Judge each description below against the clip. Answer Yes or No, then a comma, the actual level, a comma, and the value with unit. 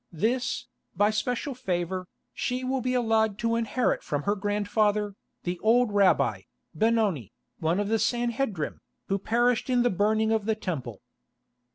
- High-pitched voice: Yes, high, 215 Hz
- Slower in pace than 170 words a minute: Yes, average, 150 wpm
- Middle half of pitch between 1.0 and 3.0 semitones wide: No, average, 3.6 semitones